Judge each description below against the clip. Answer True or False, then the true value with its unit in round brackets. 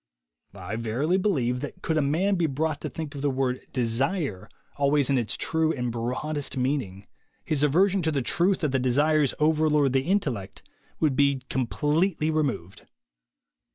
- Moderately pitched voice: True (145 Hz)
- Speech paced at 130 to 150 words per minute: False (165 wpm)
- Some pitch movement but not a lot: True (3.8 semitones)